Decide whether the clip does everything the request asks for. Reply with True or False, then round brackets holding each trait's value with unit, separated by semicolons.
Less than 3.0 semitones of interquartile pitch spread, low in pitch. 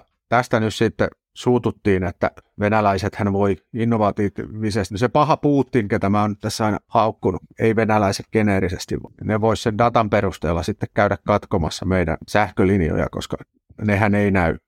True (2.6 semitones; 105 Hz)